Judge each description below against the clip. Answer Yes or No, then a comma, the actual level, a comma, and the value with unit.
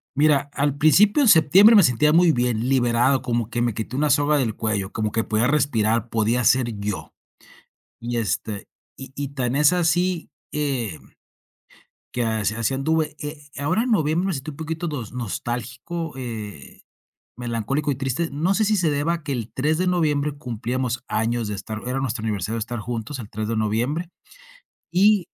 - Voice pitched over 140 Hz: No, low, 130 Hz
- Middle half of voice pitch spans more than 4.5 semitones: Yes, average, 5.0 semitones